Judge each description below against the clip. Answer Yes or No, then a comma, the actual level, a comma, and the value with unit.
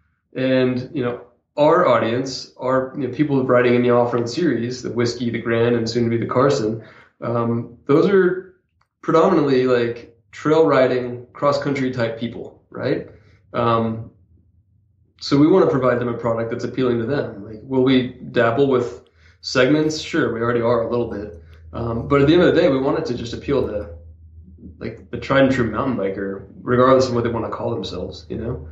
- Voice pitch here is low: Yes, low, 120 Hz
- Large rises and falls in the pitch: No, narrow, 2.4 semitones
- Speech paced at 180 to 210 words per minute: Yes, average, 200 wpm